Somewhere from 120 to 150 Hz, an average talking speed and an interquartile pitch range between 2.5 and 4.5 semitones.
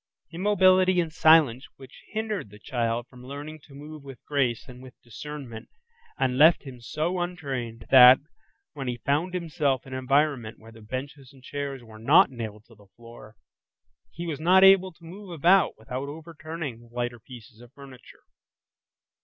No: low, 135 Hz; average, 170 wpm; average, 5.1 semitones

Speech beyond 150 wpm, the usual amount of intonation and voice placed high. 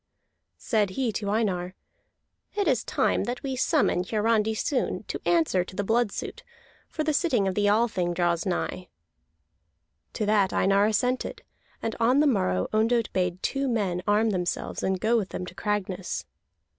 Yes: average, 165 wpm; average, 4.2 semitones; high, 210 Hz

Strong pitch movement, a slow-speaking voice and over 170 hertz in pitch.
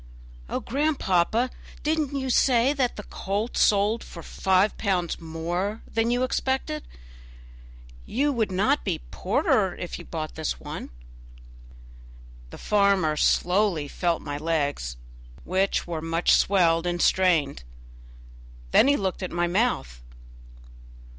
Yes: wide, 6.0 semitones; slow, 125 wpm; high, 190 Hz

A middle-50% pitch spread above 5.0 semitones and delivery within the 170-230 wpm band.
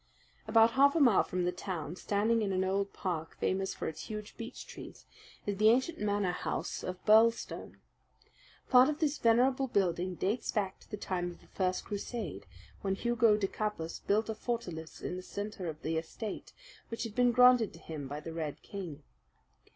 No: average, 4.3 semitones; average, 190 wpm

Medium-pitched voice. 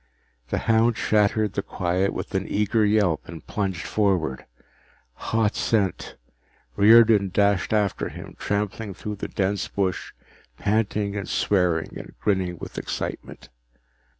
No: low, 100 Hz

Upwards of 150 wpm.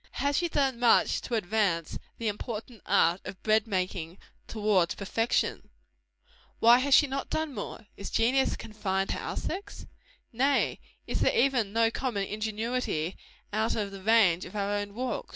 Yes: average, 160 wpm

